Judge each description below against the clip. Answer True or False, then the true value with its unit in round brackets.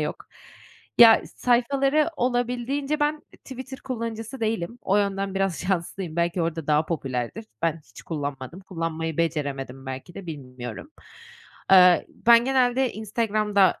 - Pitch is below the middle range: False (195 Hz)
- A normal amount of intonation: False (6.8 semitones)